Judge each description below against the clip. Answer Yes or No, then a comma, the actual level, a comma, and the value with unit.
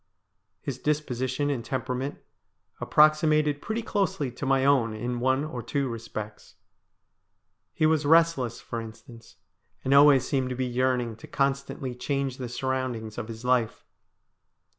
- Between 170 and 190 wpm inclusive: No, average, 140 wpm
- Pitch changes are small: No, average, 3.0 semitones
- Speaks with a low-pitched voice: Yes, low, 130 Hz